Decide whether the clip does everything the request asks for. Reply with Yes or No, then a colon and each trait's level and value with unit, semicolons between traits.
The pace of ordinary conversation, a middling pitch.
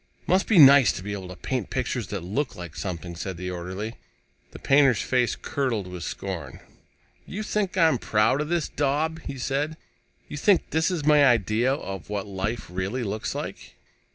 No: average, 180 wpm; low, 120 Hz